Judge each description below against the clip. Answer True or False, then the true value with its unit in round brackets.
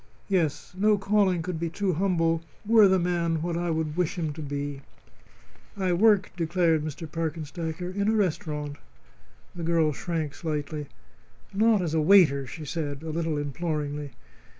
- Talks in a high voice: False (165 Hz)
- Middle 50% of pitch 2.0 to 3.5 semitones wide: True (3.1 semitones)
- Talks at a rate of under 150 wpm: False (155 wpm)